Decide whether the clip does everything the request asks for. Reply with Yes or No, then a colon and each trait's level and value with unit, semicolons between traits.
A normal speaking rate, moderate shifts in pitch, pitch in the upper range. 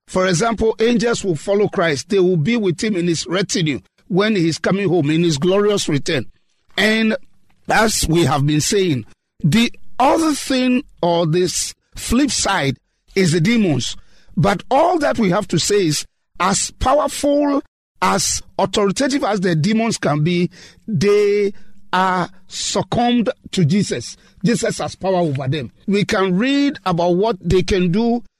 Yes: average, 155 wpm; average, 4.5 semitones; high, 195 Hz